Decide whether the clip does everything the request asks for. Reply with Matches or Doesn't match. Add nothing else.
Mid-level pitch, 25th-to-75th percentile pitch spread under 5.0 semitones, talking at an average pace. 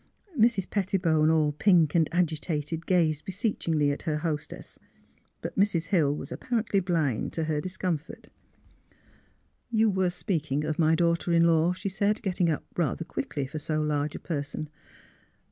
Matches